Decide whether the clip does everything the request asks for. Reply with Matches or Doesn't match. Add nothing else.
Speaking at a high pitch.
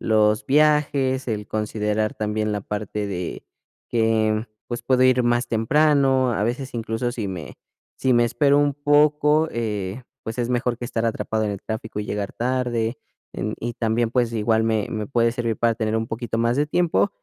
Doesn't match